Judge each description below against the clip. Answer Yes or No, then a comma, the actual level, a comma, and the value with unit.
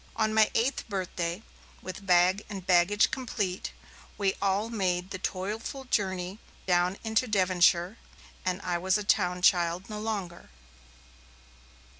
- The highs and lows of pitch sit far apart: No, average, 2.8 semitones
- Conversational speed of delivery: No, slow, 130 wpm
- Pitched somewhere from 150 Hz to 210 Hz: Yes, high, 190 Hz